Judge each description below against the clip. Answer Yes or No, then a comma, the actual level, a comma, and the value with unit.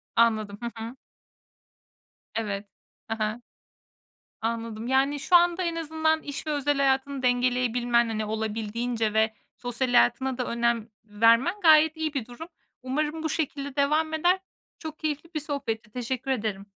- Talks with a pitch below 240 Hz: No, very high, 255 Hz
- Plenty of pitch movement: No, average, 5.0 semitones